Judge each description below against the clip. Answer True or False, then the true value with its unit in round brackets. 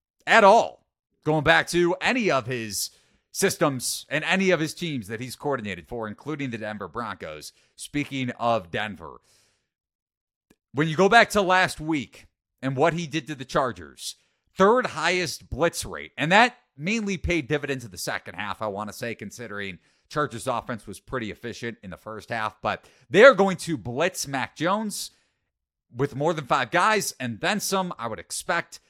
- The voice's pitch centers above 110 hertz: True (140 Hz)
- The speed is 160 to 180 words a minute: True (175 wpm)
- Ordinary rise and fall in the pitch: False (7.3 semitones)